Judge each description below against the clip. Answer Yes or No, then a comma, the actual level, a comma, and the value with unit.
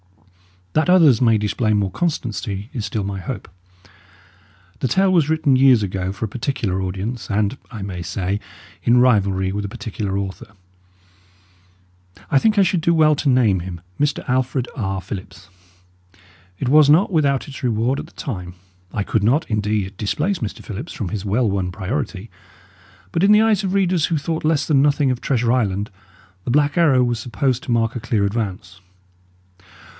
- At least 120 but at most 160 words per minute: No, average, 175 wpm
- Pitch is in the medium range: No, low, 115 Hz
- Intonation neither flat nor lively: No, wide, 6.3 semitones